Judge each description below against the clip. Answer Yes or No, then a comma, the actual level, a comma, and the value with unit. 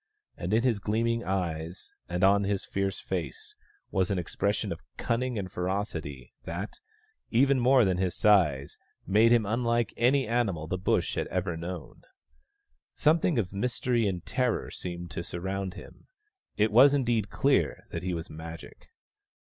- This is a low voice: Yes, low, 100 Hz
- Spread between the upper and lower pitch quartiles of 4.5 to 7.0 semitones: Yes, average, 4.8 semitones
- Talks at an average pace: Yes, average, 155 wpm